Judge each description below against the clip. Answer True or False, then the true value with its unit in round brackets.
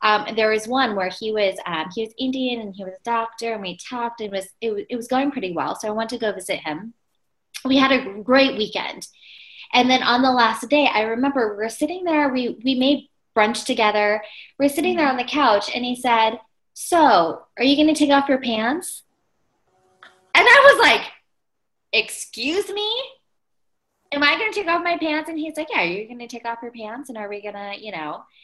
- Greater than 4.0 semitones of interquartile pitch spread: True (4.8 semitones)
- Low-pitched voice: False (240 Hz)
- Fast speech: True (230 wpm)